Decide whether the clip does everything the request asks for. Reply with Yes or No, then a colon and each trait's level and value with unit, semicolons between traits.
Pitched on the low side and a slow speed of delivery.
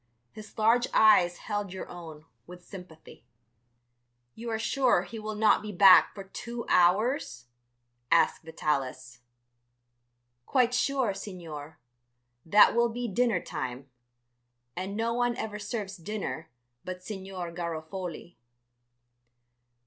No: high, 195 Hz; slow, 115 wpm